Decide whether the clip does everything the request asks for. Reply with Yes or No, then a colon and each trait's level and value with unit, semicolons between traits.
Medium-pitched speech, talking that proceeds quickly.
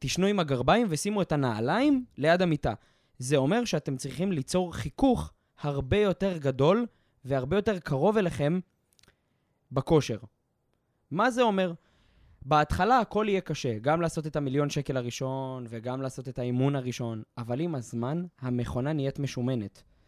No: medium, 145 Hz; average, 140 wpm